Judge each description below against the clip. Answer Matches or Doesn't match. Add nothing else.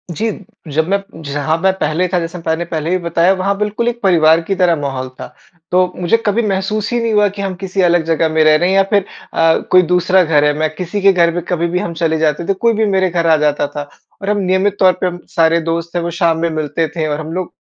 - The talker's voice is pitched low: Doesn't match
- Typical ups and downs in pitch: Matches